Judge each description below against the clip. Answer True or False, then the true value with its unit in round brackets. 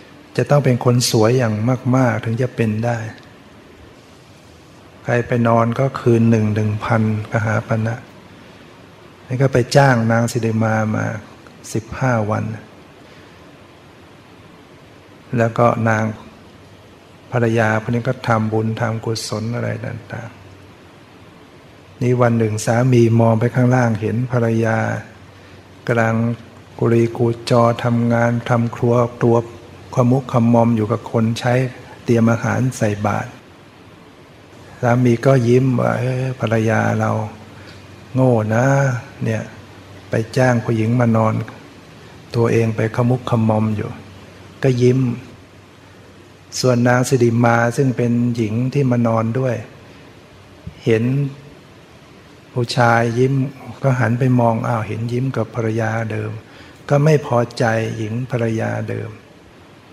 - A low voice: True (115 Hz)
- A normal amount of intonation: False (2.0 semitones)